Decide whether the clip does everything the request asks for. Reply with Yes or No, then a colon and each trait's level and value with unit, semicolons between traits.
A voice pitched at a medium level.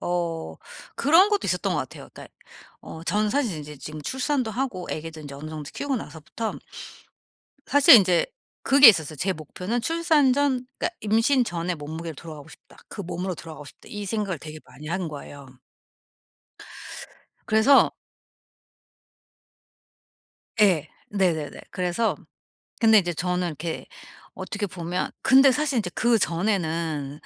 Yes: medium, 180 Hz